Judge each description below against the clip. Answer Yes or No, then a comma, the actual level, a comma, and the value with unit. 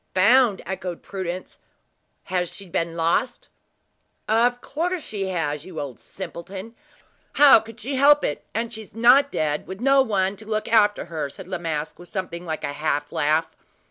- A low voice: No, high, 190 Hz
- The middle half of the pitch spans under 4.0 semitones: No, average, 5.3 semitones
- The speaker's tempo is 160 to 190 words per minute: Yes, average, 170 wpm